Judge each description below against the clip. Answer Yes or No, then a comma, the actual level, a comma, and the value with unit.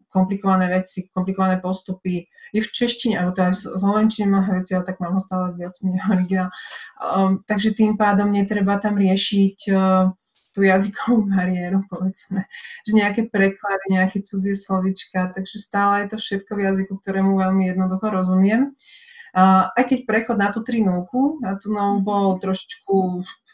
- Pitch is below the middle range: No, high, 195 Hz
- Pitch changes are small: Yes, narrow, 1.8 semitones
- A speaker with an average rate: Yes, average, 160 wpm